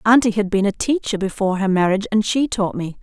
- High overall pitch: Yes, high, 205 Hz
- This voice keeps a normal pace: No, fast, 240 wpm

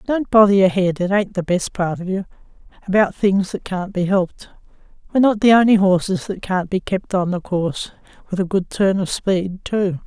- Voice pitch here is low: No, high, 190 Hz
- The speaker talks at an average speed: Yes, average, 195 wpm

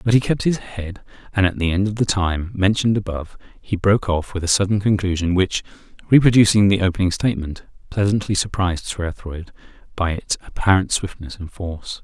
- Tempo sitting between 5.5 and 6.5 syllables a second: Yes, 6.0 syllables/s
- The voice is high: No, very low, 95 Hz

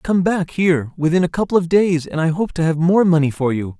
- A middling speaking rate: No, fast, 270 wpm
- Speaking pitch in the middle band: Yes, medium, 165 Hz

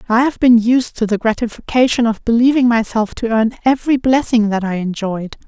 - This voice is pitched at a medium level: No, high, 230 Hz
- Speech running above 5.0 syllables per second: Yes, 5.5 syllables/s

